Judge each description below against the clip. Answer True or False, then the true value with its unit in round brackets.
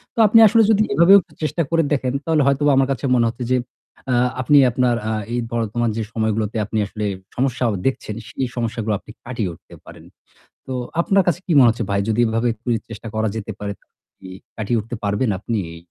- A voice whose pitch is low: True (120 Hz)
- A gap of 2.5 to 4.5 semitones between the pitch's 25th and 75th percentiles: True (3.7 semitones)